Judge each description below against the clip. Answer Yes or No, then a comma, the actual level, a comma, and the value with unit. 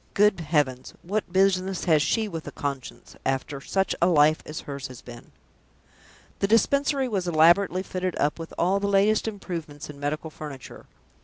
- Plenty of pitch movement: No, average, 5.0 semitones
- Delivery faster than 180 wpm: No, average, 165 wpm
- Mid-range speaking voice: Yes, medium, 170 Hz